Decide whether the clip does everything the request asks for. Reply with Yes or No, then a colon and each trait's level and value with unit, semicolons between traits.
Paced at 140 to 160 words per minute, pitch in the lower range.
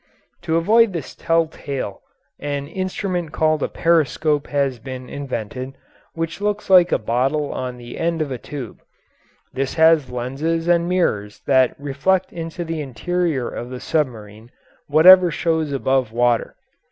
No: average, 145 wpm; medium, 150 Hz